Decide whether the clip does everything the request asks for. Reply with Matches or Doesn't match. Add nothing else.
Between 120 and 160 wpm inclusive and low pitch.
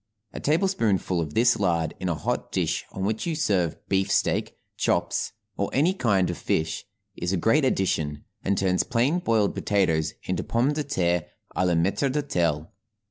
Doesn't match